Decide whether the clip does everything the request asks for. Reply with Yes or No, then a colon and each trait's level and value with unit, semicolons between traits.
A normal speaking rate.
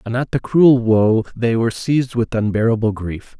Yes: average, 195 wpm